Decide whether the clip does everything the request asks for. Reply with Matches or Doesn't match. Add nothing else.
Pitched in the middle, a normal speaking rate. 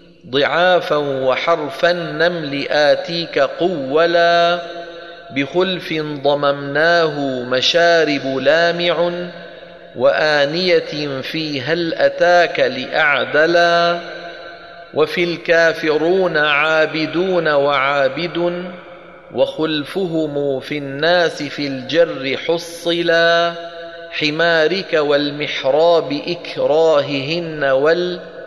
Doesn't match